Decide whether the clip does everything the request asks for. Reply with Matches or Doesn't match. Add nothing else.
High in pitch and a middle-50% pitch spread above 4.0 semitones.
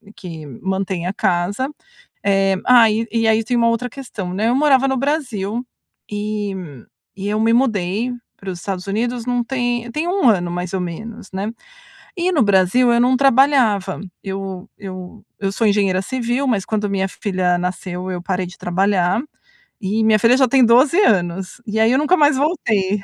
Matches